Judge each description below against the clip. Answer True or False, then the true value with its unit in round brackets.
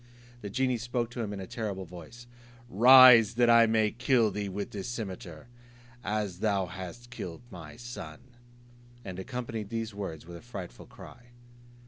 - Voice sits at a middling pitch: False (110 Hz)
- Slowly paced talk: False (160 wpm)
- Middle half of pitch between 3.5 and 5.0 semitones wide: True (4.1 semitones)